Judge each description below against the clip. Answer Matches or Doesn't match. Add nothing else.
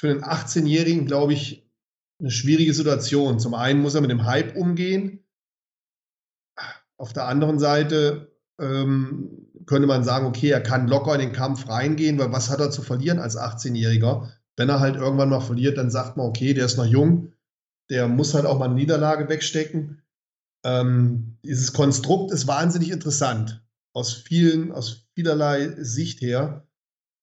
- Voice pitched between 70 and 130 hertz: Doesn't match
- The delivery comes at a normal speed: Matches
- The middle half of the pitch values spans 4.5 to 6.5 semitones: Doesn't match